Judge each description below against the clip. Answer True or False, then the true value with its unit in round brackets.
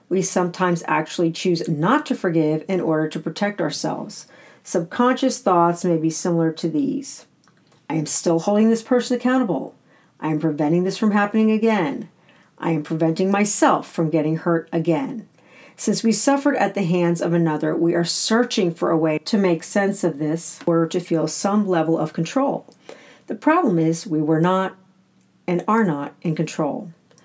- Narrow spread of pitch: False (4.4 semitones)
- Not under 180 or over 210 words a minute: False (170 wpm)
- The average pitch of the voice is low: False (180 Hz)